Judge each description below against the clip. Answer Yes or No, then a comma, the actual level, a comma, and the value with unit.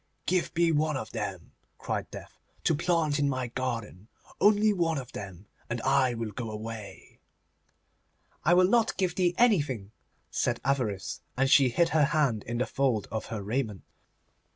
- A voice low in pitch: Yes, low, 130 Hz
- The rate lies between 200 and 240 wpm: No, average, 165 wpm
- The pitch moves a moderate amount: No, wide, 6.7 semitones